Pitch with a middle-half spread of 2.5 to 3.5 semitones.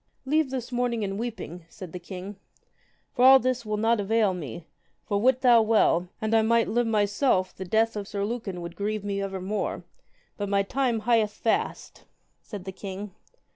Yes: average, 3.2 semitones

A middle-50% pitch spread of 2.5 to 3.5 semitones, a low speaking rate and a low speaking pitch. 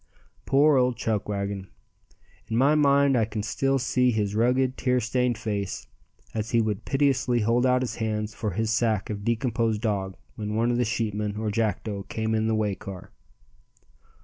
No: average, 2.9 semitones; average, 175 wpm; low, 110 Hz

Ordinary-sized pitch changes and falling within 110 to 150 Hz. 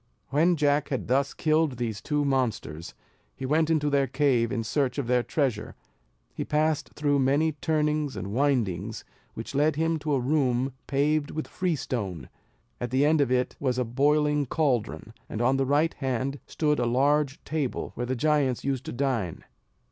Yes: average, 3.2 semitones; medium, 140 Hz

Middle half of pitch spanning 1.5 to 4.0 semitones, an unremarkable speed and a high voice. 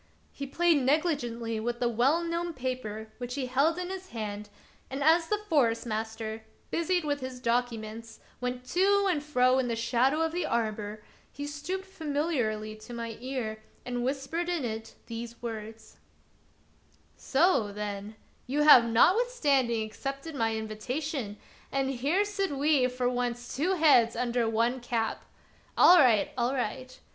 No: average, 4.8 semitones; average, 155 wpm; very high, 250 Hz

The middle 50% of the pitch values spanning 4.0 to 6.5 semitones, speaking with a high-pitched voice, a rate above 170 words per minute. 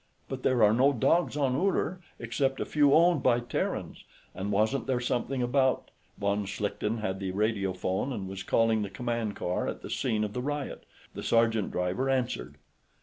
No: average, 4.5 semitones; low, 120 Hz; average, 190 wpm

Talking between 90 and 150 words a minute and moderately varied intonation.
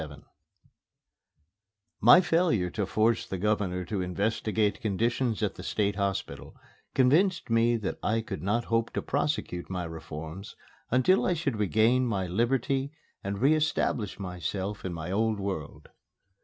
Yes: average, 140 wpm; average, 4.3 semitones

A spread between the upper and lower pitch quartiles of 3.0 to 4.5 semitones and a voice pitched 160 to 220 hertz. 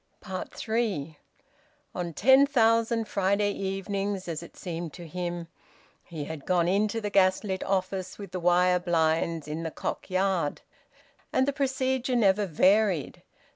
Yes: average, 3.5 semitones; high, 190 Hz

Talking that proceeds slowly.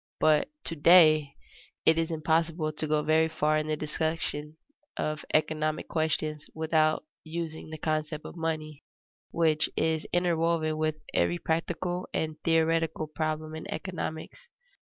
Yes: slow, 130 wpm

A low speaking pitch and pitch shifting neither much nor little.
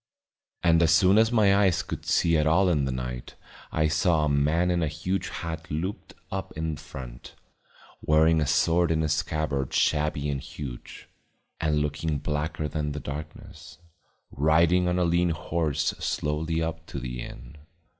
No: very low, 80 Hz; narrow, 2.2 semitones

